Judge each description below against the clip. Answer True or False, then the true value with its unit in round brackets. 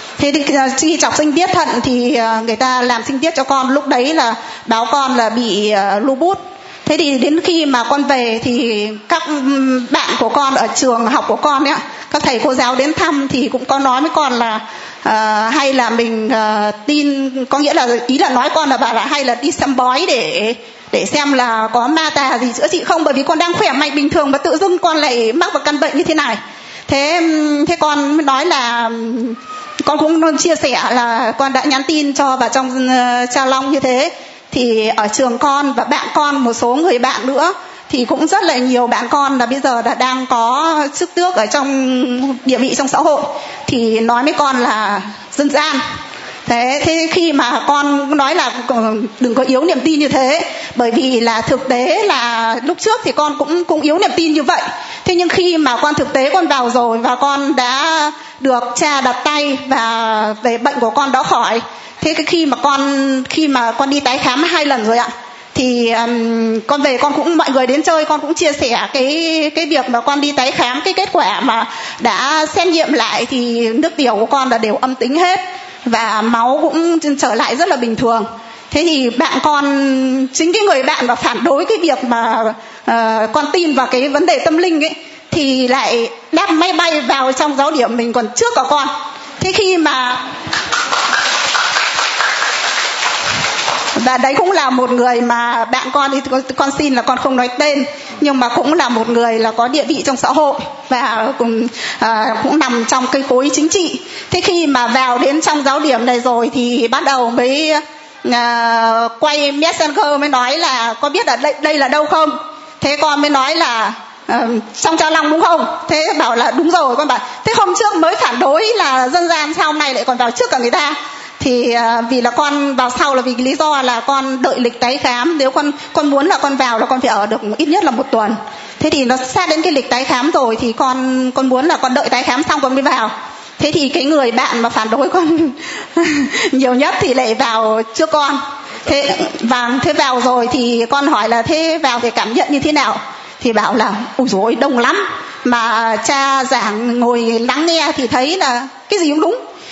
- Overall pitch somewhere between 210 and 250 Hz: False (275 Hz)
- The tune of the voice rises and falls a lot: False (4.1 semitones)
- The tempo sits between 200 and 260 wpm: True (215 wpm)